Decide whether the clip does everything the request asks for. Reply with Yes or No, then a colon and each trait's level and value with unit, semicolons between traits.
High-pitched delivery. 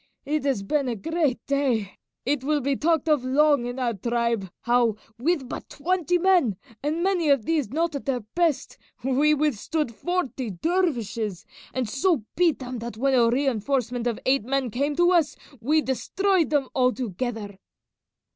Yes: very high, 270 Hz